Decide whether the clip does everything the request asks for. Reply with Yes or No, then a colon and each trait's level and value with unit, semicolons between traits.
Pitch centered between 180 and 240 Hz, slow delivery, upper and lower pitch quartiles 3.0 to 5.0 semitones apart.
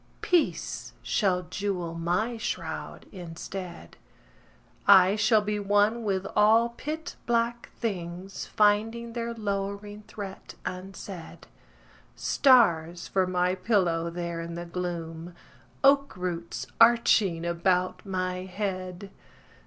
Yes: high, 190 Hz; slow, 105 wpm; average, 3.5 semitones